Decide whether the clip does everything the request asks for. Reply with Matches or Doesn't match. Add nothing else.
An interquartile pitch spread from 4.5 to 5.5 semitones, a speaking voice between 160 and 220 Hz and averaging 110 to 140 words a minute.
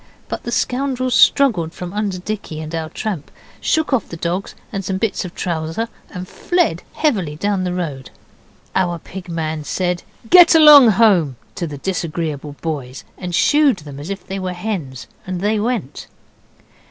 Doesn't match